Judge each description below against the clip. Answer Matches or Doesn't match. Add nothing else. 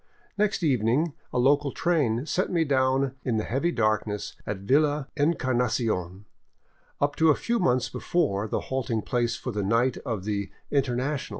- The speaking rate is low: Doesn't match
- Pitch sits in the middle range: Doesn't match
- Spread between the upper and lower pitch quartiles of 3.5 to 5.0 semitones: Matches